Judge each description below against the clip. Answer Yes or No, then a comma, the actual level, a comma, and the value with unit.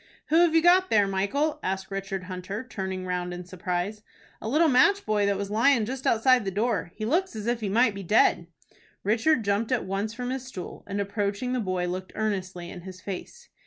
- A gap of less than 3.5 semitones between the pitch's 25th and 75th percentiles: No, average, 4.8 semitones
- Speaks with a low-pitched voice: No, high, 205 Hz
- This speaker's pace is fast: Yes, fast, 210 wpm